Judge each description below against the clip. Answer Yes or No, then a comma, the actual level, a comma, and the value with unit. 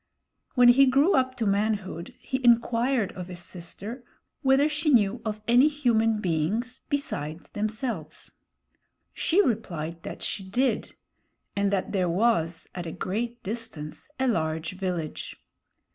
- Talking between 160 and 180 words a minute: No, slow, 135 wpm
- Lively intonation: Yes, wide, 5.7 semitones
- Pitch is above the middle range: Yes, high, 215 Hz